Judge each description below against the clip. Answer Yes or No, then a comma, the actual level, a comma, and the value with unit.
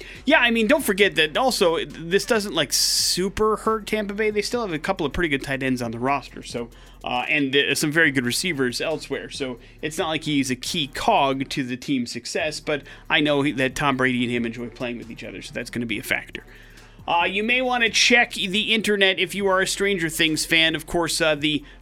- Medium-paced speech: No, fast, 240 wpm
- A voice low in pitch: No, medium, 155 Hz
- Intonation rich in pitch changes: Yes, wide, 6.9 semitones